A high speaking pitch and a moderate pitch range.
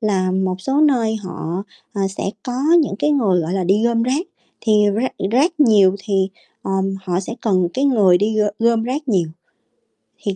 Yes: high, 210 Hz; average, 4.7 semitones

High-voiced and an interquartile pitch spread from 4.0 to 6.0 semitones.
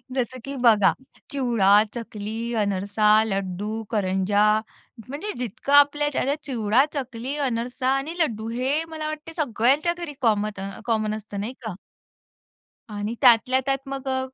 Yes: high, 235 Hz; average, 4.5 semitones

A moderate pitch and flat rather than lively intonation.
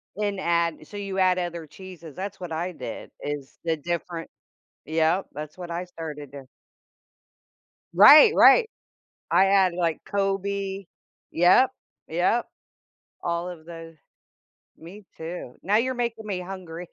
No: medium, 180 Hz; average, 3.1 semitones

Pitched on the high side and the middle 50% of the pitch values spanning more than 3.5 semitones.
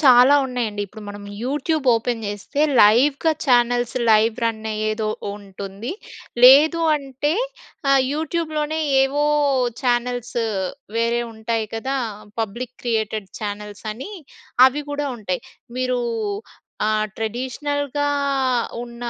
Yes: high, 240 Hz; average, 4.2 semitones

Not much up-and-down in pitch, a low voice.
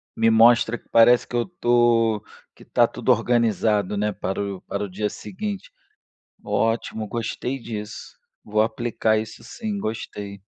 Yes: narrow, 2.3 semitones; low, 115 Hz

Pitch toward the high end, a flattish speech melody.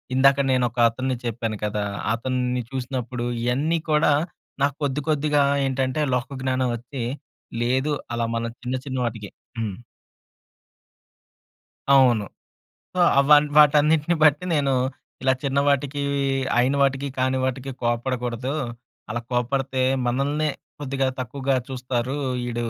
No: low, 130 Hz; narrow, 2.3 semitones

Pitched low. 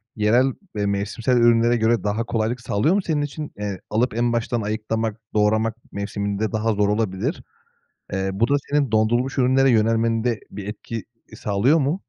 Yes: low, 115 Hz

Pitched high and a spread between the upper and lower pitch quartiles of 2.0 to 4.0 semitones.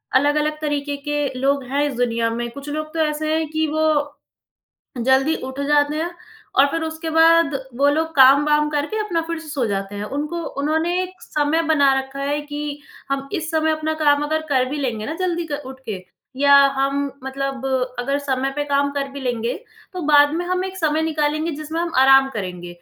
Yes: very high, 290 Hz; average, 2.7 semitones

